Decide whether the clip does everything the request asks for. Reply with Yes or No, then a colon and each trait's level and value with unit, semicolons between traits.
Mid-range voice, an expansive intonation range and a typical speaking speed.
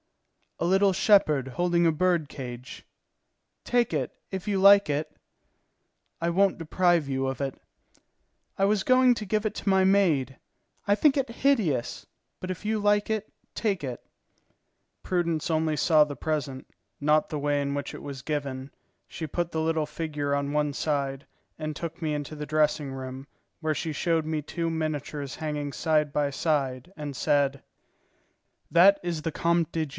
No: medium, 155 Hz; average, 4.2 semitones; average, 170 wpm